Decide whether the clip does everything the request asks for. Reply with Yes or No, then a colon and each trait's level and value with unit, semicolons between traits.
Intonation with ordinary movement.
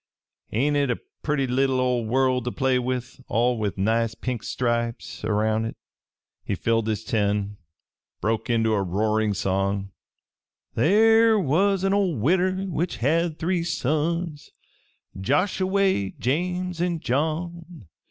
No: wide, 7.5 semitones